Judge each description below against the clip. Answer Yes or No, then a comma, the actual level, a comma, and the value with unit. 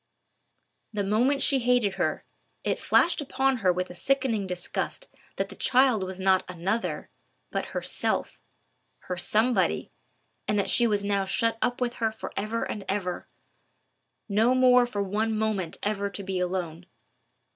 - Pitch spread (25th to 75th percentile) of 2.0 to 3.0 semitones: No, average, 4.3 semitones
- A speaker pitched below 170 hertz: No, high, 210 Hz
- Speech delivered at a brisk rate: No, average, 155 wpm